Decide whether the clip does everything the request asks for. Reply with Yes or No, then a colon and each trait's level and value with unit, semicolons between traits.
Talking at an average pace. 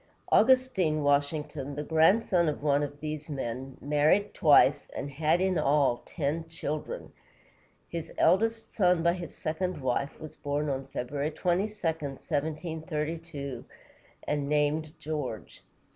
No: slow, 125 wpm